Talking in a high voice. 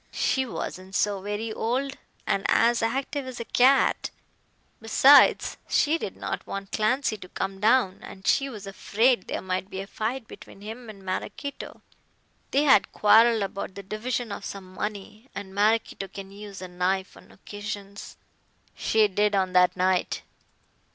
Yes: high, 210 Hz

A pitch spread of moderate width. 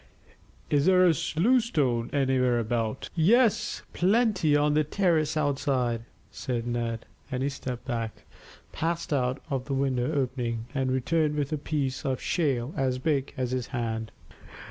Yes: average, 3.9 semitones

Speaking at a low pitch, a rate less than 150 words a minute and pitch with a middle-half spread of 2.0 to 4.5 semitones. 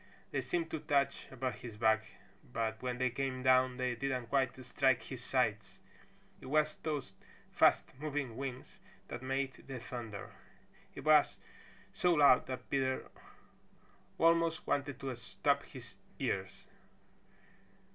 Yes: low, 130 Hz; slow, 135 wpm; narrow, 2.4 semitones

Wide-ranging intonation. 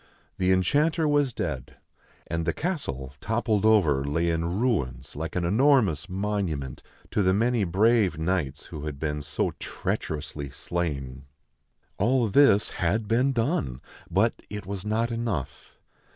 Yes: wide, 7.1 semitones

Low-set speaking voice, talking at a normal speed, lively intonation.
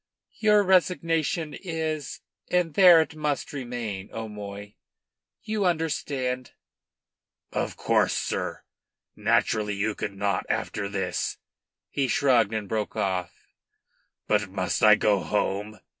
No: low, 120 Hz; slow, 115 wpm; wide, 7.8 semitones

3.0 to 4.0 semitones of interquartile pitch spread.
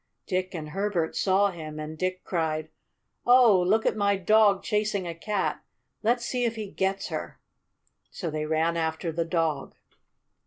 No: average, 4.4 semitones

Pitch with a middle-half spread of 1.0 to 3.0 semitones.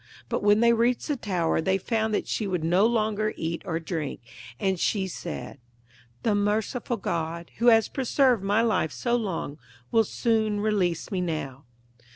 No: average, 4.8 semitones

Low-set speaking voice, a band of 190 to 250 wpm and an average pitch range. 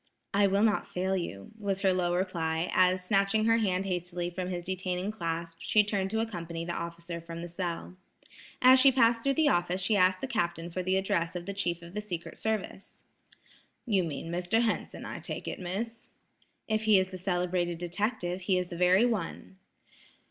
No: medium, 185 Hz; average, 195 wpm; average, 3.0 semitones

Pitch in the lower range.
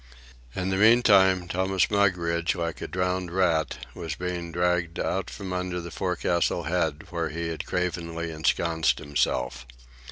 Yes: very low, 85 Hz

